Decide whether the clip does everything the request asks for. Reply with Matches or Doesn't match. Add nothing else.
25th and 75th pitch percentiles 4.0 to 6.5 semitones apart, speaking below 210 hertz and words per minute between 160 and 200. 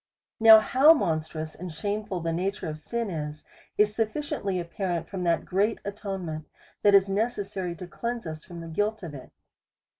Matches